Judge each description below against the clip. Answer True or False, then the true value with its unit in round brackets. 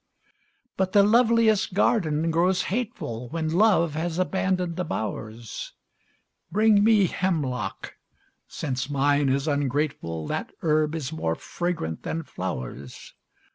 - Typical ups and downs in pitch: False (5.8 semitones)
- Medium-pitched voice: True (160 Hz)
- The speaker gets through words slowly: True (115 wpm)